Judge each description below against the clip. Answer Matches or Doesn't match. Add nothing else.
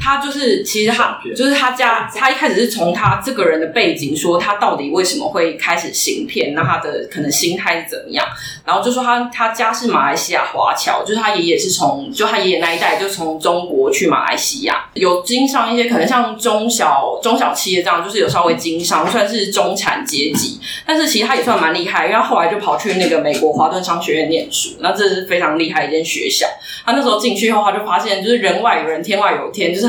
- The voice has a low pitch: Doesn't match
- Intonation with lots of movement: Matches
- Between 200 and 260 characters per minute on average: Doesn't match